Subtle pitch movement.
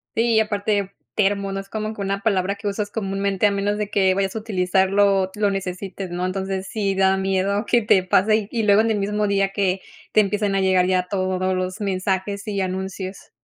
Yes: narrow, 1.5 semitones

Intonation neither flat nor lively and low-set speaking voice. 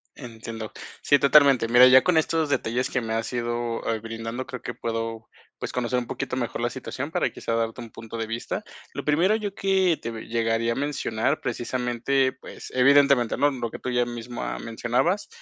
Yes: average, 3.2 semitones; low, 120 Hz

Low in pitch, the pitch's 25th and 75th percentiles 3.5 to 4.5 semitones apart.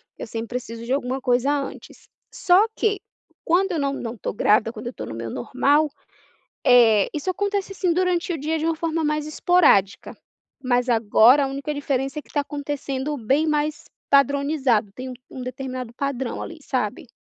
No: very high, 275 Hz; average, 3.8 semitones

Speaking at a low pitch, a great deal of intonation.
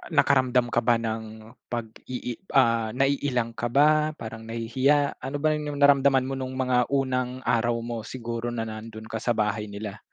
No: low, 120 Hz; average, 2.9 semitones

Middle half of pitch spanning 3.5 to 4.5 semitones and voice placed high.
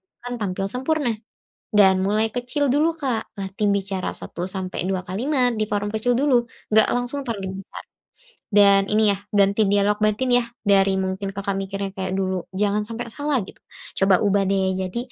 Yes: average, 3.8 semitones; high, 205 Hz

